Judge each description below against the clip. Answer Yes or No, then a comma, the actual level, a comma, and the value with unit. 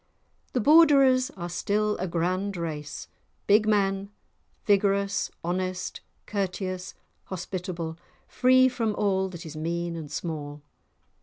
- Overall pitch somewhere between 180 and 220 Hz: Yes, high, 190 Hz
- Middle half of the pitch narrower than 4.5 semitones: Yes, average, 3.5 semitones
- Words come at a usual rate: No, slow, 110 wpm